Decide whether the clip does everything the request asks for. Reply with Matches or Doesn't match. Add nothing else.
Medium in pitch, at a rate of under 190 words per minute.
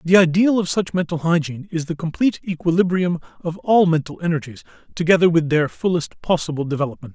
Matches